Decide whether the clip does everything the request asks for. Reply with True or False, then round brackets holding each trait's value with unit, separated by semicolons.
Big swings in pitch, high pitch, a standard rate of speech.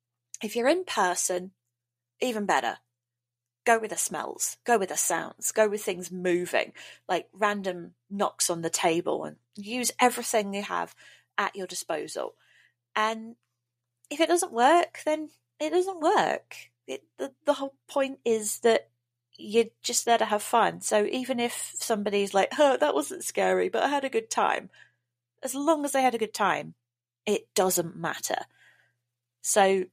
True (6.7 semitones; 205 Hz; 160 wpm)